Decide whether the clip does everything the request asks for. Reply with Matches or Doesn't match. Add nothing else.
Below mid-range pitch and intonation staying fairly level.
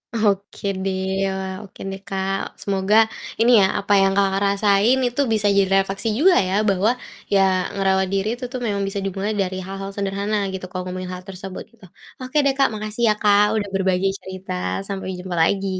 Doesn't match